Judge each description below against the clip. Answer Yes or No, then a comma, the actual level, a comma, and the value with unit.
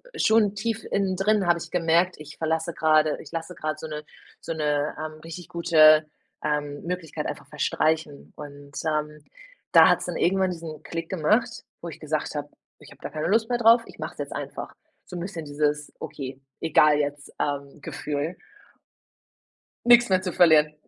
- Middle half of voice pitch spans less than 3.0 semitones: No, average, 3.3 semitones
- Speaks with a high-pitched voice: No, medium, 160 Hz